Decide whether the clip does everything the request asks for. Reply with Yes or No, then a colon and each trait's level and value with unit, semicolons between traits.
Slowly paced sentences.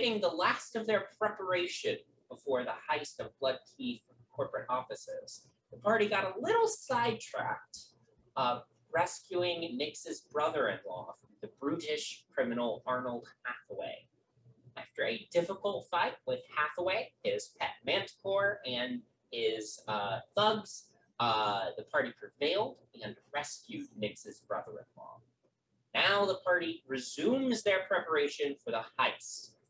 Yes: slow, 125 wpm